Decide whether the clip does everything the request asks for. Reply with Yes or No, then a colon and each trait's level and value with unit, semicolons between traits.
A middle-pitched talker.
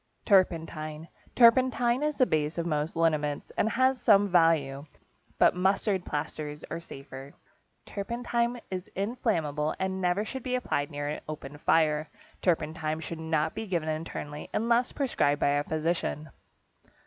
Yes: medium, 165 Hz